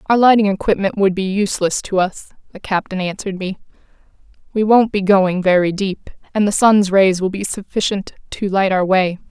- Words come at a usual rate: Yes, average, 185 wpm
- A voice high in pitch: Yes, high, 195 Hz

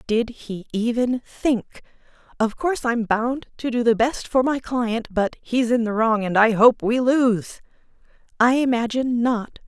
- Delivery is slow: No, average, 175 wpm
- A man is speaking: No, female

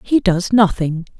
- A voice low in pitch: No, high, 190 Hz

